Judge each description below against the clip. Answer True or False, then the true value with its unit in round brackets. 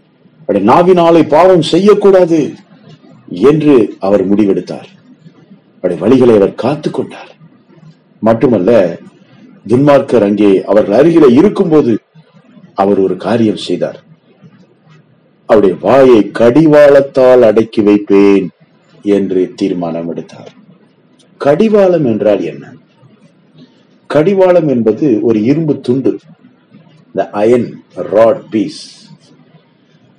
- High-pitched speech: False (125 Hz)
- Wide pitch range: True (8.5 semitones)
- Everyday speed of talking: False (70 wpm)